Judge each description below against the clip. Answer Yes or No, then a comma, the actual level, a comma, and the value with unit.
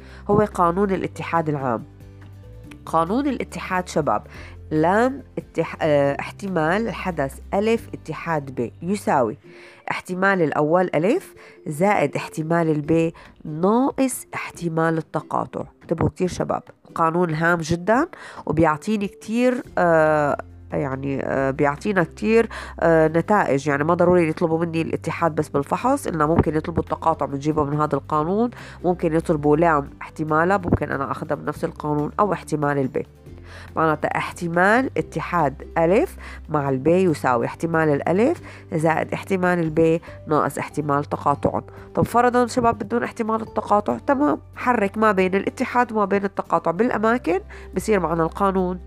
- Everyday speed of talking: Yes, average, 120 wpm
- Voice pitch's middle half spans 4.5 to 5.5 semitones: Yes, average, 5.2 semitones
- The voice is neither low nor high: Yes, medium, 165 Hz